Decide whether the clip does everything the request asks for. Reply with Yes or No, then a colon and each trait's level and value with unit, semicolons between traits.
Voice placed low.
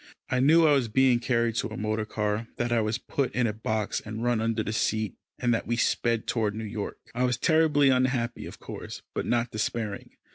Yes: low, 115 Hz